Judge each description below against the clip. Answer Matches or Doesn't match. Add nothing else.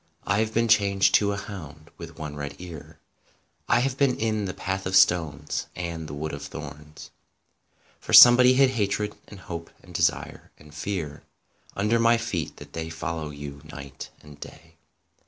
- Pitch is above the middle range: Doesn't match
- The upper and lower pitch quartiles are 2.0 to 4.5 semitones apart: Doesn't match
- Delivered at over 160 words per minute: Matches